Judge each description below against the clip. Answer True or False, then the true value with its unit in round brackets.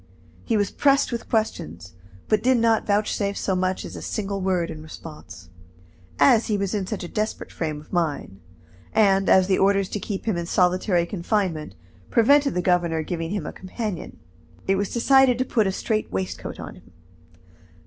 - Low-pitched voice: False (195 Hz)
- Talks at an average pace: True (180 wpm)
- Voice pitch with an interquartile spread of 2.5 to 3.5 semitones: False (4.0 semitones)